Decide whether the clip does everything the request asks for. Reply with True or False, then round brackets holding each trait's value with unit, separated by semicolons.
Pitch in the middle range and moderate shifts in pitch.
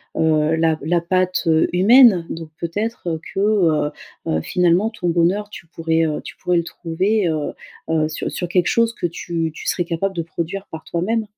True (170 Hz; 3.0 semitones)